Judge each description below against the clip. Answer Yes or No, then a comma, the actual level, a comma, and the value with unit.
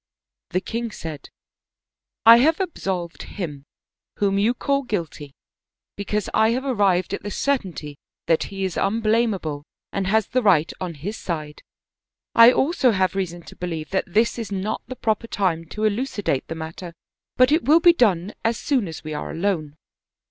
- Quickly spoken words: No, average, 175 wpm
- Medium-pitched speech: No, high, 195 Hz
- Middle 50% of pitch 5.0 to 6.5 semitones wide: Yes, wide, 5.5 semitones